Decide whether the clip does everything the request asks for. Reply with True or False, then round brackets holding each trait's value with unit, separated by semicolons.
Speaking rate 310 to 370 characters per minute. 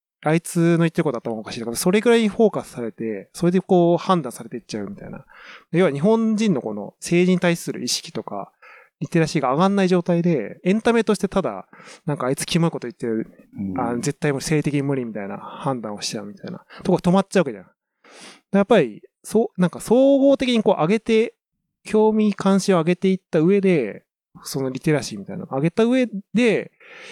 False (425 characters per minute)